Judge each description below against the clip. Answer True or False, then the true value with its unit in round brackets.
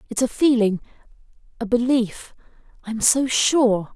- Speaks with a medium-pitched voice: False (235 Hz)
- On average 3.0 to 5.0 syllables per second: True (4.5 syllables/s)